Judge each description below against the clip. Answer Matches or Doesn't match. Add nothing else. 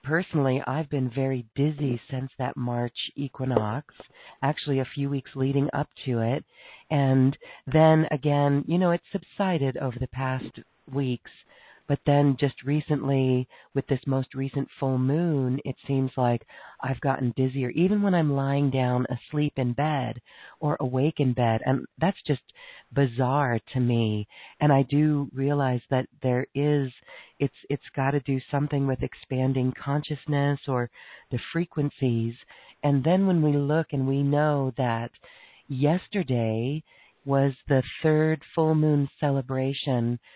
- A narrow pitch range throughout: Matches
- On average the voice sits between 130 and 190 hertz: Matches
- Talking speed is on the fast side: Doesn't match